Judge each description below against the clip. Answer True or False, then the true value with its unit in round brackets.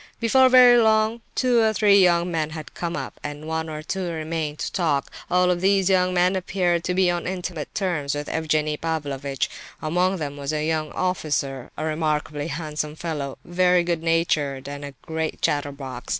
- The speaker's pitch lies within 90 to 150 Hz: False (160 Hz)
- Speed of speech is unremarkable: True (180 wpm)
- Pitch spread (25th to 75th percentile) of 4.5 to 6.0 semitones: False (3.4 semitones)